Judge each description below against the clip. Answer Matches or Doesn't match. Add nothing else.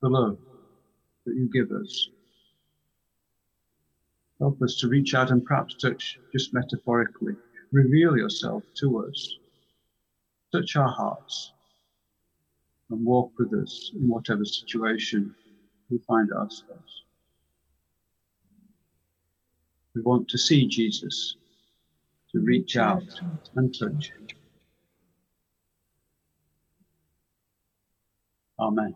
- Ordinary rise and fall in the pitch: Doesn't match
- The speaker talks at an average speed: Doesn't match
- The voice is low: Matches